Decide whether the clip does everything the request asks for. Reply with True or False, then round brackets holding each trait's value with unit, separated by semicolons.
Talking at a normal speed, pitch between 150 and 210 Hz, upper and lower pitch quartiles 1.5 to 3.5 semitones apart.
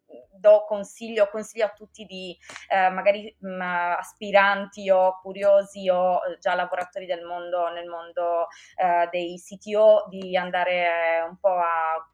True (135 wpm; 185 Hz; 2.5 semitones)